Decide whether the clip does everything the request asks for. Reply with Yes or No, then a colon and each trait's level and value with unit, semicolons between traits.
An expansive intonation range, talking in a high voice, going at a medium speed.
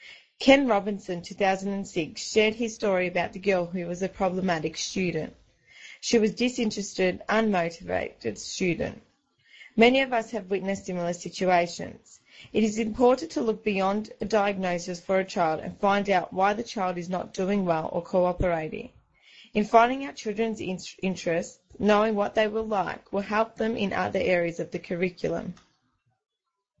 No: average, 3.4 semitones; high, 195 Hz; average, 155 wpm